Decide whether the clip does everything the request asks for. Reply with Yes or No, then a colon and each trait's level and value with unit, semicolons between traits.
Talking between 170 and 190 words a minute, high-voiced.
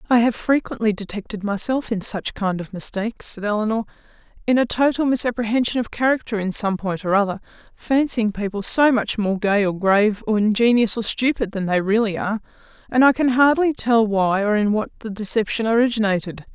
Yes: average, 185 wpm; high, 220 Hz